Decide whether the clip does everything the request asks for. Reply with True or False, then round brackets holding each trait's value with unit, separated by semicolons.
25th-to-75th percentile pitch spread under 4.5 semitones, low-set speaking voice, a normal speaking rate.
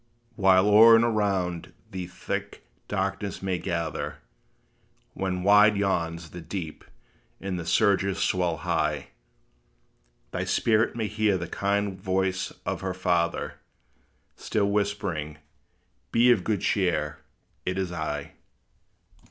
False (2.9 semitones; 95 Hz; 120 wpm)